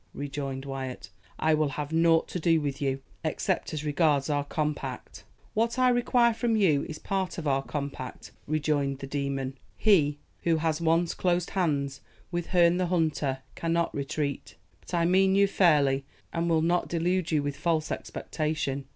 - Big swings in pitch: No, average, 3.5 semitones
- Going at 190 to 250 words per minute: No, average, 170 wpm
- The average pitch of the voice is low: No, medium, 155 Hz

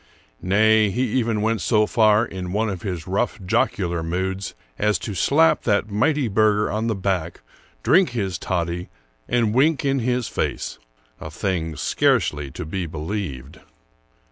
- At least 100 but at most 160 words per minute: Yes, average, 155 wpm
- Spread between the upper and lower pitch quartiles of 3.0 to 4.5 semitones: Yes, average, 4.1 semitones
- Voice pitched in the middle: No, low, 100 Hz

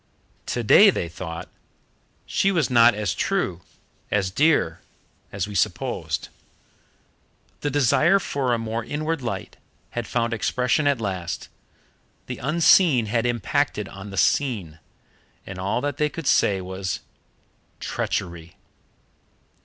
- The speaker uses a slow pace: Yes, slow, 120 wpm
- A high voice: No, low, 115 Hz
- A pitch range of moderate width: No, wide, 7.0 semitones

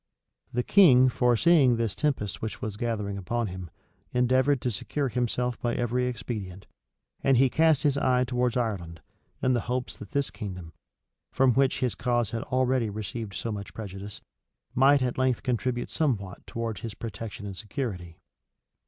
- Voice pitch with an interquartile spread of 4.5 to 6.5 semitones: No, average, 3.6 semitones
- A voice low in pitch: Yes, low, 120 Hz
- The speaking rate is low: No, average, 155 wpm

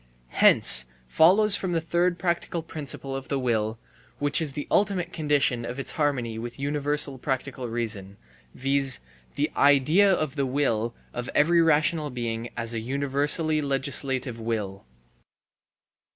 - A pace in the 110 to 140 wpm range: Yes, slow, 135 wpm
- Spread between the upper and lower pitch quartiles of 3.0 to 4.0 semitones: No, average, 4.4 semitones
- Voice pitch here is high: No, medium, 140 Hz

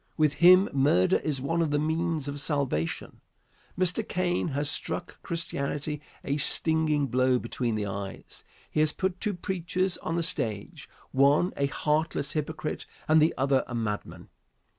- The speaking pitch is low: No, medium, 150 Hz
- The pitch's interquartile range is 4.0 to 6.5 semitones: No, average, 3.5 semitones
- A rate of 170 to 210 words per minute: No, average, 155 wpm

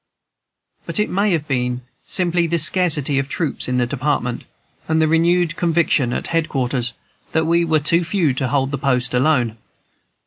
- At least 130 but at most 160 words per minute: No, average, 175 wpm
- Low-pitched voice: No, medium, 155 Hz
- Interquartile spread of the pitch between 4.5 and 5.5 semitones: Yes, average, 4.8 semitones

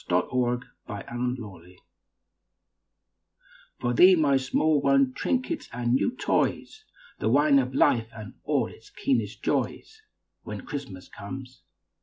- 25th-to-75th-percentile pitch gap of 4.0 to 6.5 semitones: No, average, 3.3 semitones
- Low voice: Yes, low, 125 Hz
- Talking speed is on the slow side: Yes, slow, 120 wpm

